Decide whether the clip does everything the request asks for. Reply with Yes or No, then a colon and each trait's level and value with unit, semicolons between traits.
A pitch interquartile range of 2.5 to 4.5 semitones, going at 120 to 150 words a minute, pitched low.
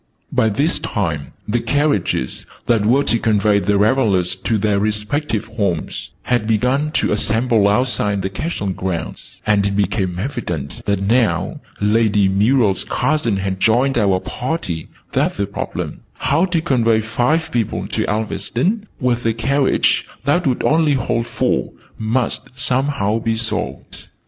Yes: average, 4.2 semitones; average, 145 wpm; low, 110 Hz